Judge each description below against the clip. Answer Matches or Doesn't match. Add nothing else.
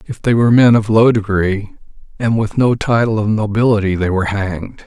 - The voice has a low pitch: Matches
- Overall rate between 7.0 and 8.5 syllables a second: Doesn't match